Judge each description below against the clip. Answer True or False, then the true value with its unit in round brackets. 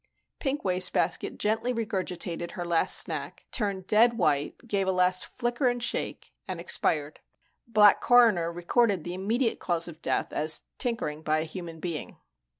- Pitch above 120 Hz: True (185 Hz)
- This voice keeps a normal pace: True (150 wpm)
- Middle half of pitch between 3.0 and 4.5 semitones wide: False (5.3 semitones)